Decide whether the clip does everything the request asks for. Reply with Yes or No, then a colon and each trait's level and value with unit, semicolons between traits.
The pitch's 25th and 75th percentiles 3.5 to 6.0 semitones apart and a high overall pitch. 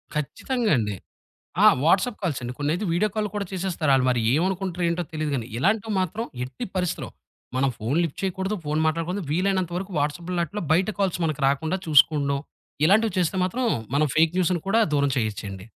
No: average, 4.8 semitones; medium, 170 Hz